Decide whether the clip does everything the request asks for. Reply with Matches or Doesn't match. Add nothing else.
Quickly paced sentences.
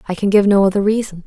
Matches